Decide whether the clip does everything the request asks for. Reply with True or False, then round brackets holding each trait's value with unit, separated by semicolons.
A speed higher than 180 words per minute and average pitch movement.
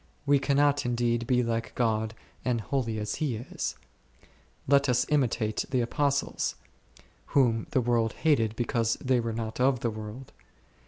False (150 wpm; 3.0 semitones)